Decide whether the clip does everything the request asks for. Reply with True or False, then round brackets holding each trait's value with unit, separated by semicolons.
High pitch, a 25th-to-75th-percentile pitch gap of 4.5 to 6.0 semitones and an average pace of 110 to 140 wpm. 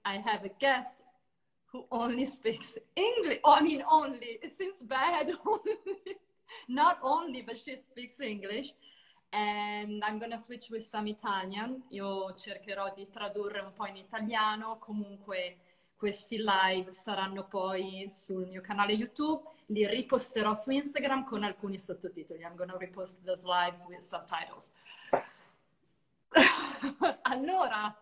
True (215 Hz; 5.3 semitones; 135 wpm)